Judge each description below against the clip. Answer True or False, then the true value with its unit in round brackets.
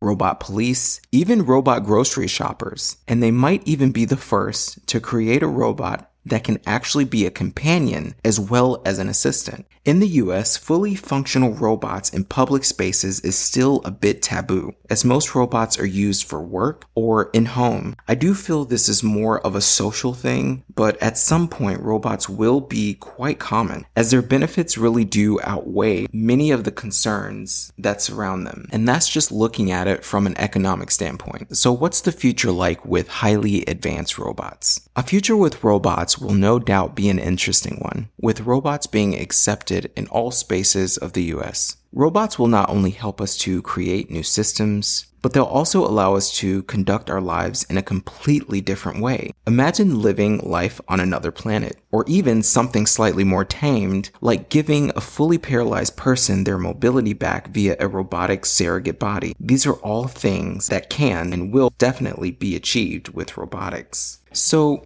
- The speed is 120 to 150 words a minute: False (175 wpm)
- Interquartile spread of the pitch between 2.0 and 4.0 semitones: False (5.0 semitones)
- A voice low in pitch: True (110 Hz)